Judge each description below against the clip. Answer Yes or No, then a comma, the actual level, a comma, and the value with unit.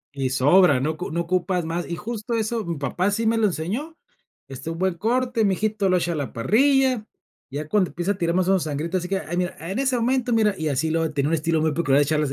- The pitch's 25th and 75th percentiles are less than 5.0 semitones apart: No, wide, 5.4 semitones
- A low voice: No, medium, 180 Hz